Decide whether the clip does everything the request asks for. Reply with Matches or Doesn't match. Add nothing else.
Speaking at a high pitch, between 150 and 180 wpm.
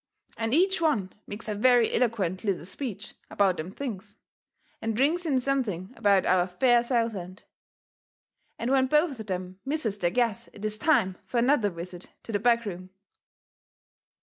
Matches